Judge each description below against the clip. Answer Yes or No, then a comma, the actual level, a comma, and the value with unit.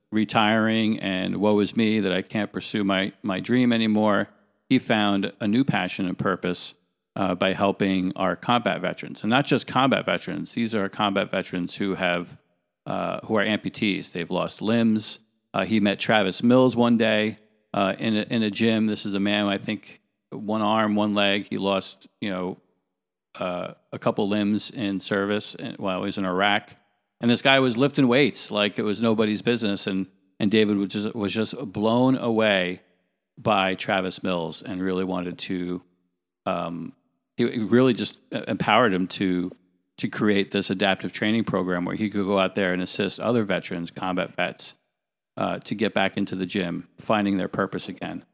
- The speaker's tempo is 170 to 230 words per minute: Yes, average, 180 wpm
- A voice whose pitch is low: Yes, low, 100 Hz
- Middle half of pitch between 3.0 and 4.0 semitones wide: No, narrow, 2.6 semitones